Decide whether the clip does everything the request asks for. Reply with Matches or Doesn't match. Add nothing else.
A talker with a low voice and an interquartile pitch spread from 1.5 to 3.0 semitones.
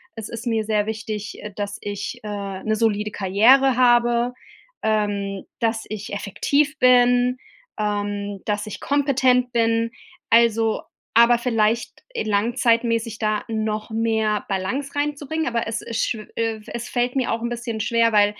Doesn't match